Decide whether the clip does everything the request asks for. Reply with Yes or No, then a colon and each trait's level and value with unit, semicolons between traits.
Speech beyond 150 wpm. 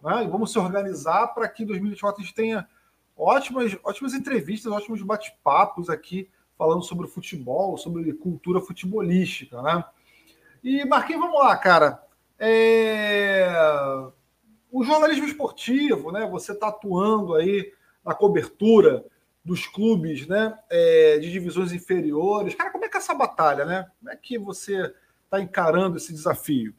No: average, 145 wpm